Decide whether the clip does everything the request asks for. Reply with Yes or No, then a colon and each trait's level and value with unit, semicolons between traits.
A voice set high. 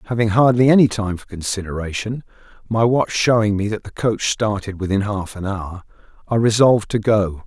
No: low, 105 Hz